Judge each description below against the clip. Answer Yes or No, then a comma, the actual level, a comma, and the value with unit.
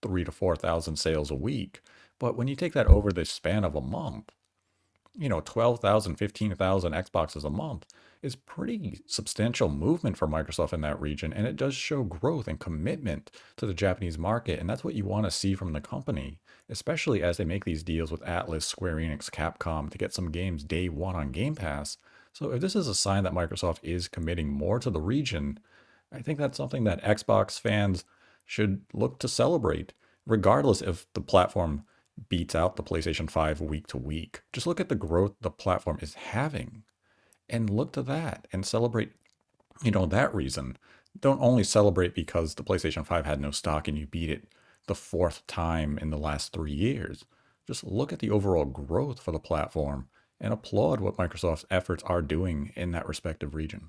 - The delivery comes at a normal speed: Yes, average, 190 wpm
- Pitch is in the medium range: No, very low, 90 Hz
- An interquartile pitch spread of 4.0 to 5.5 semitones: Yes, average, 5.2 semitones